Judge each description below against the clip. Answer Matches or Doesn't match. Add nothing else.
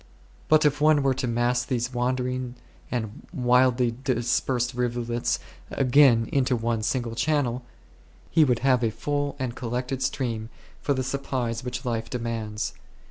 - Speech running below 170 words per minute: Matches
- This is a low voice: Matches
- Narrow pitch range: Matches